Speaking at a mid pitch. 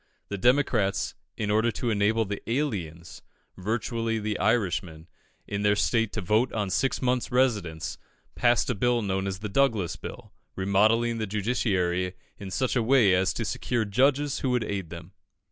No: low, 105 Hz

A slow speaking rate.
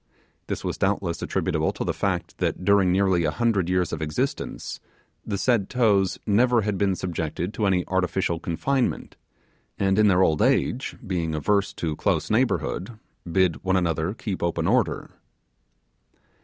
No: average, 155 wpm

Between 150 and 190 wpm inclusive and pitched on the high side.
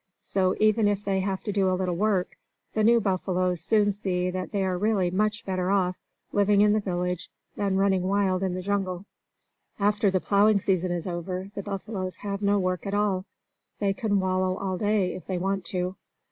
No: average, 200 wpm; high, 195 Hz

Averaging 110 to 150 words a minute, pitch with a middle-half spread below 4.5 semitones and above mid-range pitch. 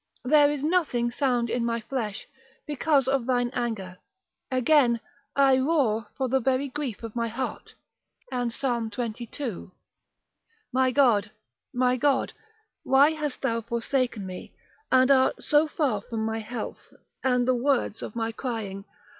Yes: average, 145 wpm; average, 2.9 semitones; very high, 250 Hz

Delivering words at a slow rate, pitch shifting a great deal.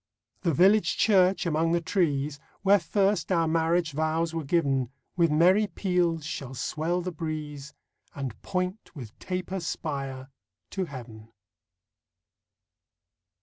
No: slow, 120 wpm; average, 4.1 semitones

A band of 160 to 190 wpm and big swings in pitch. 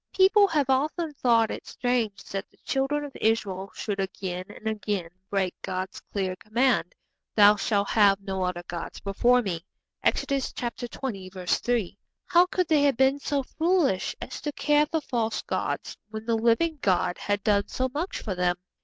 Yes: average, 170 wpm; wide, 6.0 semitones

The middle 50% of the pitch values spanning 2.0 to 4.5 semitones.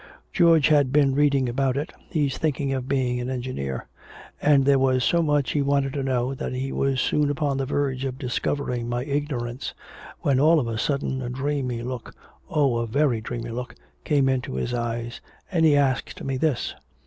Yes: narrow, 2.6 semitones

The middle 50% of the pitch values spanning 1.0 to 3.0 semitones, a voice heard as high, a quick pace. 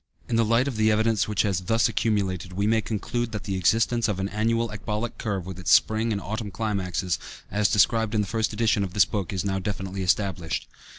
No: average, 2.7 semitones; low, 105 Hz; fast, 220 wpm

